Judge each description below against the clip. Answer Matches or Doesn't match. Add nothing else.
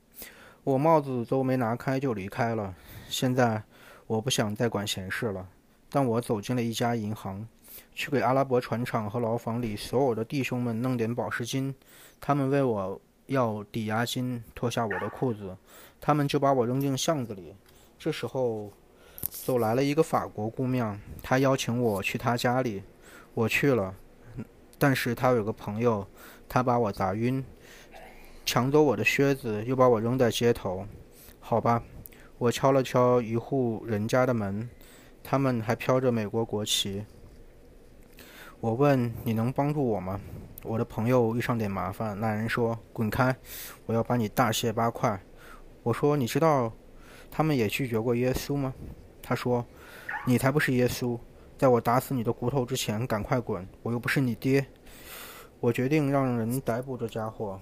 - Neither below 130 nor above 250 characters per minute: Matches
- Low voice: Matches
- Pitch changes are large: Doesn't match